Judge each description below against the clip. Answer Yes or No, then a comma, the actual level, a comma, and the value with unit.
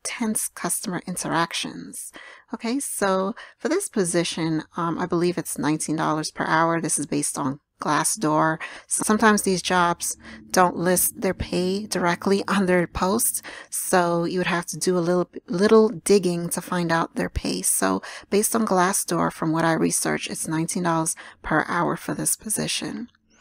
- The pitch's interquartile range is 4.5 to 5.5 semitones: No, average, 3.4 semitones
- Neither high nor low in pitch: Yes, medium, 180 Hz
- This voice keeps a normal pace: Yes, average, 155 wpm